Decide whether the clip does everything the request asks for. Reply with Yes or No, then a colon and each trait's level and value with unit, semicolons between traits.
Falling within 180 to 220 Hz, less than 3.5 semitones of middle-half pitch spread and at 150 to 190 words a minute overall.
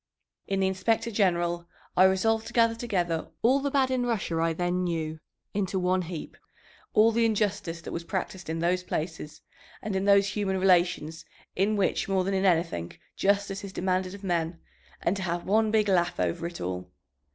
Yes: high, 190 Hz; average, 3.0 semitones; average, 185 wpm